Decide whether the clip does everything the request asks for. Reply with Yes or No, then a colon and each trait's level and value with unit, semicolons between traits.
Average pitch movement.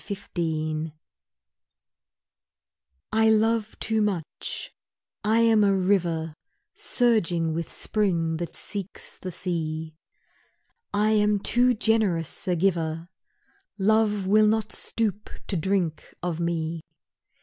Yes: average, 4.6 semitones